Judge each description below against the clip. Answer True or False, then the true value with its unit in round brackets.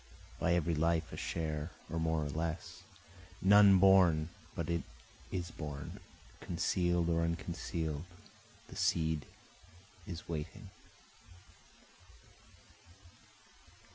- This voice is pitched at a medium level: False (85 Hz)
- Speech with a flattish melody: True (1.7 semitones)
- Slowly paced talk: True (95 wpm)